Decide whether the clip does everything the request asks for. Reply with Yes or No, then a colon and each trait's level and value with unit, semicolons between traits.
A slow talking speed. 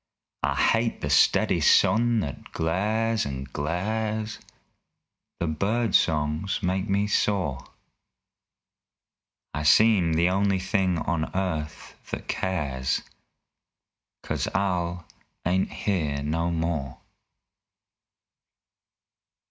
Yes: slow, 90 wpm